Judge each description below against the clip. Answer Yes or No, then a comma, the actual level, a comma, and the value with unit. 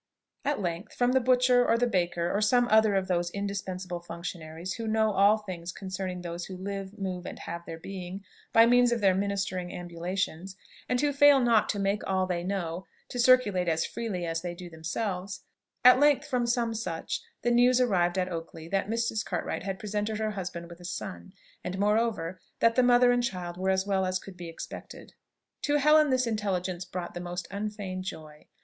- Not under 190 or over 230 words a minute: Yes, average, 195 wpm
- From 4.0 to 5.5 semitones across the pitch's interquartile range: Yes, average, 4.3 semitones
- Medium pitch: No, high, 195 Hz